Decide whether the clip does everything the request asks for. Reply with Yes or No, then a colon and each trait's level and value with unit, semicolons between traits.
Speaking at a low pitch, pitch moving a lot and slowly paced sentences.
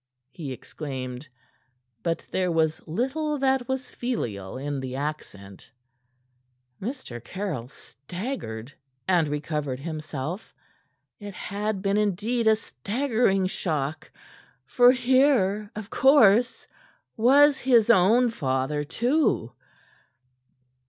No: high, 190 Hz; wide, 8.9 semitones; slow, 100 wpm